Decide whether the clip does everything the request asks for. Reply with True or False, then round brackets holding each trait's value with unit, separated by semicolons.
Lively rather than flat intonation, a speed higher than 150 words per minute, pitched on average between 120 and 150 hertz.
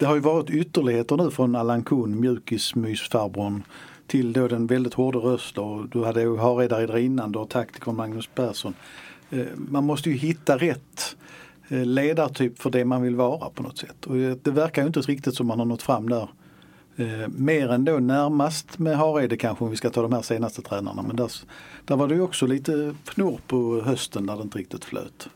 False (3.8 semitones; 195 wpm; 125 Hz)